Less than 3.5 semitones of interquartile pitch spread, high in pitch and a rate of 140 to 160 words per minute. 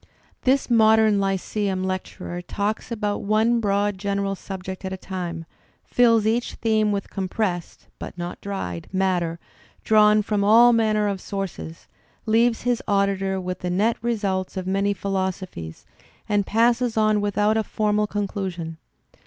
Yes: narrow, 2.4 semitones; high, 200 Hz; average, 145 wpm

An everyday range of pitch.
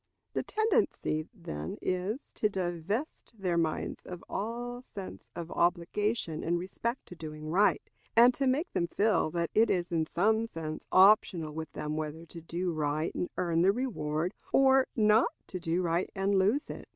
Yes: average, 4.8 semitones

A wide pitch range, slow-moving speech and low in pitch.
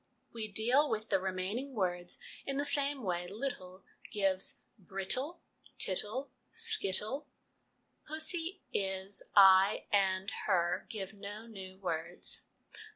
No: wide, 6.1 semitones; slow, 110 wpm; high, 205 Hz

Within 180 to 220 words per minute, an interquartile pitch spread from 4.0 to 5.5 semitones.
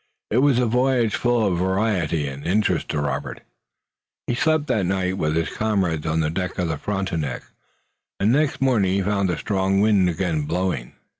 Yes: average, 190 wpm; average, 4.7 semitones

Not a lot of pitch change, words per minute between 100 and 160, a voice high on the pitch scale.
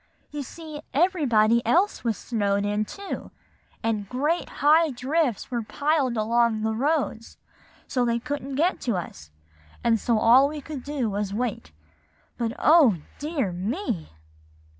No: average, 5.3 semitones; average, 145 wpm; high, 245 Hz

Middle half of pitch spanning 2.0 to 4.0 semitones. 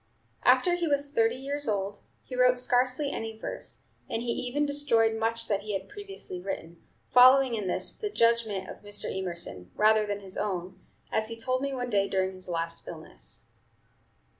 No: average, 4.7 semitones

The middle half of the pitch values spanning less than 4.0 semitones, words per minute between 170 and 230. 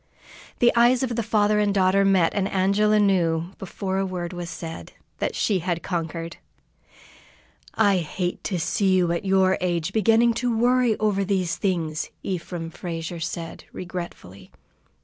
No: average, 3.3 semitones; average, 150 wpm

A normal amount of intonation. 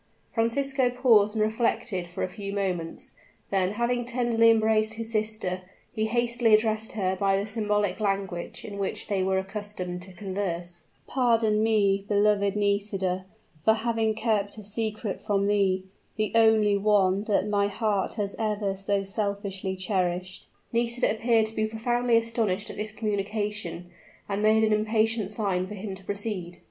No: narrow, 2.2 semitones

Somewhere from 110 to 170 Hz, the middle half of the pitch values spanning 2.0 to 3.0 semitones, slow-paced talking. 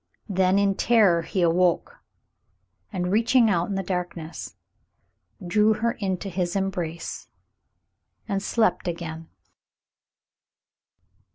No: high, 190 Hz; average, 2.7 semitones; slow, 100 wpm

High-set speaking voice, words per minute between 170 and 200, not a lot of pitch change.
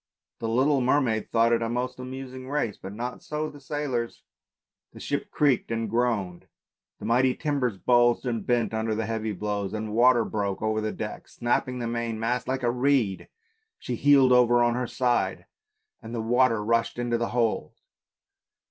No: low, 120 Hz; average, 175 wpm; narrow, 2.2 semitones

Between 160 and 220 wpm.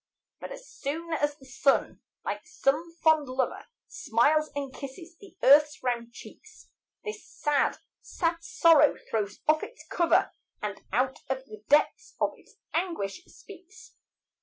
No: average, 140 wpm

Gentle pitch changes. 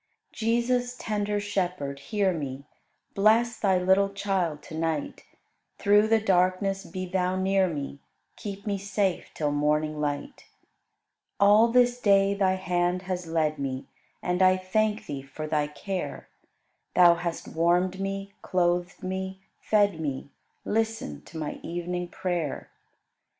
No: average, 3.5 semitones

